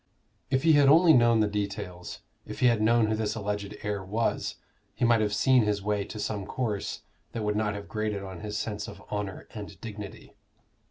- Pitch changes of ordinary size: No, narrow, 2.1 semitones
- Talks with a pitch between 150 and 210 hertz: No, low, 105 Hz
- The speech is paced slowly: No, fast, 205 wpm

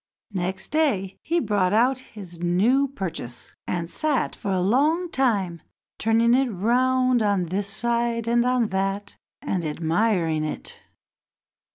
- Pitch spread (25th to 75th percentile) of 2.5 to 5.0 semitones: No, wide, 5.4 semitones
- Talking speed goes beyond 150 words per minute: No, slow, 135 wpm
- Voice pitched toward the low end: No, high, 210 Hz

